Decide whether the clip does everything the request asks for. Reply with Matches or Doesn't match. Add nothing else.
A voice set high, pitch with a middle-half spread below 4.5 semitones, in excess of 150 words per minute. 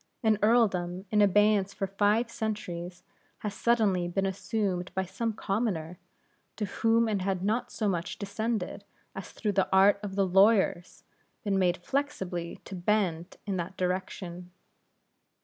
Doesn't match